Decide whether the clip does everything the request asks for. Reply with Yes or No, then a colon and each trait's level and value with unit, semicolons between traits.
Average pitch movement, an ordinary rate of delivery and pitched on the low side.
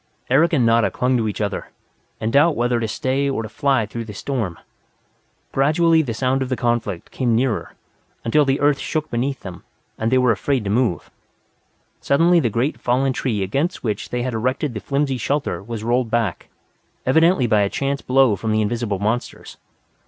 Yes: average, 3.7 semitones; average, 190 wpm; low, 125 Hz